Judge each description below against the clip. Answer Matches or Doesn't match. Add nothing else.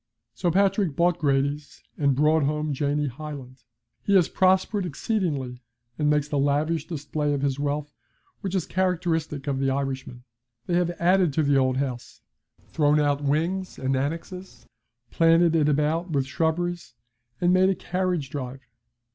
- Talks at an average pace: Matches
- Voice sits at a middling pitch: Matches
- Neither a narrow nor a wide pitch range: Matches